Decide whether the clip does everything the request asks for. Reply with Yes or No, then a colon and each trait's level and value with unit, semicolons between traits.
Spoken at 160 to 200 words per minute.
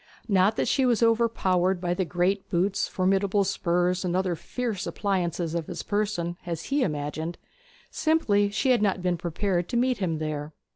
Yes: average, 175 wpm